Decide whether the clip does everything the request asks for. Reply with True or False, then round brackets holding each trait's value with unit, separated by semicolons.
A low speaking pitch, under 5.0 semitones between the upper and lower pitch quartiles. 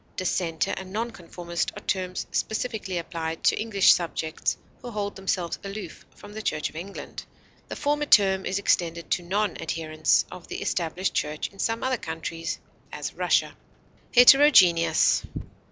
False (185 Hz; 4.1 semitones)